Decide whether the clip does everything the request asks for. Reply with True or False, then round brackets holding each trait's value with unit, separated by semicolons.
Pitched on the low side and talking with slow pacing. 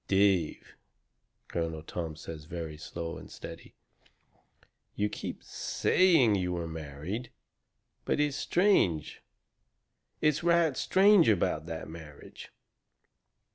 True (90 Hz; 100 wpm)